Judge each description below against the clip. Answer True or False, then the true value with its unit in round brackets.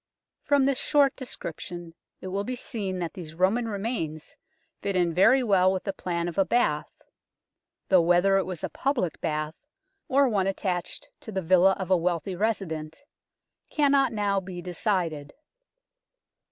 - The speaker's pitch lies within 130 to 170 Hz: False (190 Hz)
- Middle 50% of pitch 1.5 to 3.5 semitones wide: False (4.1 semitones)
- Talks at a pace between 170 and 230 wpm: False (155 wpm)